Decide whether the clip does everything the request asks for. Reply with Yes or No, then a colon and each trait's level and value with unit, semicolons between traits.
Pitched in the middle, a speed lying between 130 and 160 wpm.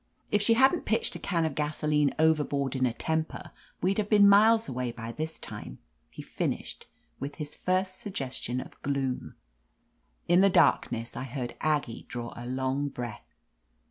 No: medium, 150 Hz; average, 170 wpm